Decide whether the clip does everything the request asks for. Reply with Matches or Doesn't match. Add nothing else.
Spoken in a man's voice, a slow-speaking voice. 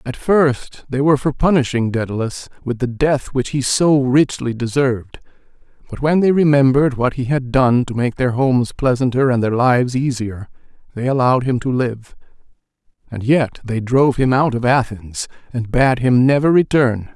Doesn't match